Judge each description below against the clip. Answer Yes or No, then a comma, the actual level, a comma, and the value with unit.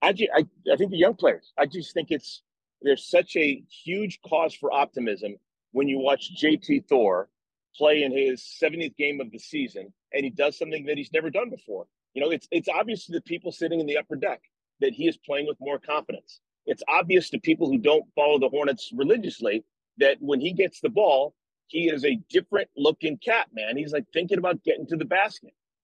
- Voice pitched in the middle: Yes, medium, 160 Hz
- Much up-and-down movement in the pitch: Yes, wide, 6.4 semitones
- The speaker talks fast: Yes, fast, 215 wpm